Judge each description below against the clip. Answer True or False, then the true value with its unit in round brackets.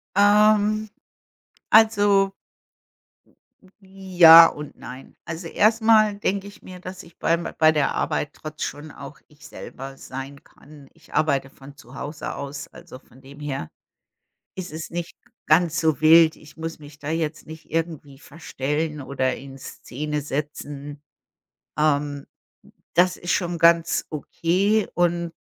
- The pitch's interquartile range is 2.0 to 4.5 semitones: True (3.7 semitones)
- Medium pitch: True (160 Hz)